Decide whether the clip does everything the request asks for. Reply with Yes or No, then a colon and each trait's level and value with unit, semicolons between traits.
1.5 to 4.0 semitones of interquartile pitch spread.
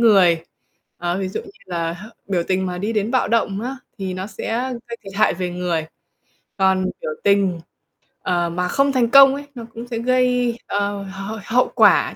No: average, 4.6 semitones